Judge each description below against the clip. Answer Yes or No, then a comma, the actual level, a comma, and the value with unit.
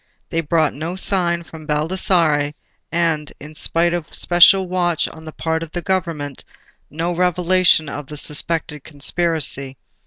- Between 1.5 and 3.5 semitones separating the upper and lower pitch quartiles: Yes, narrow, 2.6 semitones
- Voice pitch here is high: No, medium, 165 Hz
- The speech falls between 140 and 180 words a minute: Yes, average, 145 wpm